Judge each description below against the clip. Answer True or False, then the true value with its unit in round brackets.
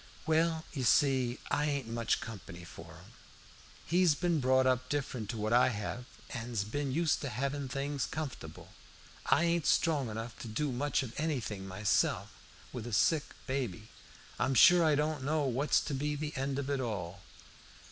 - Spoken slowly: False (175 wpm)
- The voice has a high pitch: False (135 Hz)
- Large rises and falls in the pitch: False (4.2 semitones)